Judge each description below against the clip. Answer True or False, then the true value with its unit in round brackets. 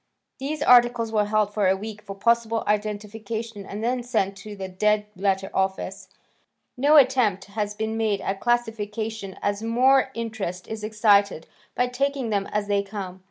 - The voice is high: True (215 Hz)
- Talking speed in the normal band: True (160 wpm)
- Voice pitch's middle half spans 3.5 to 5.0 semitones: False (2.5 semitones)